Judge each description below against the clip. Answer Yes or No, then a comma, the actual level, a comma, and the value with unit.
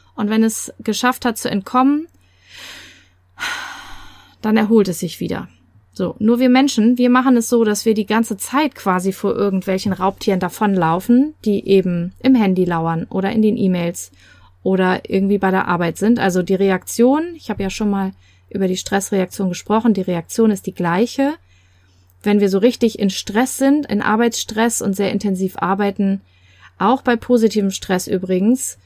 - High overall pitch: Yes, high, 200 Hz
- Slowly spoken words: No, average, 165 wpm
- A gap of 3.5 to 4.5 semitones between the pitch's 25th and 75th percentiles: Yes, average, 3.9 semitones